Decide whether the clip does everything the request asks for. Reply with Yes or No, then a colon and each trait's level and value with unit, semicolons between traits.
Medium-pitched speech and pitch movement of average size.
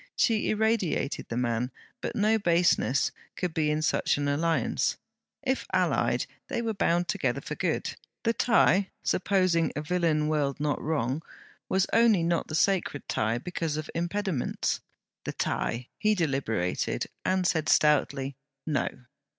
Yes: medium, 165 Hz; average, 5.0 semitones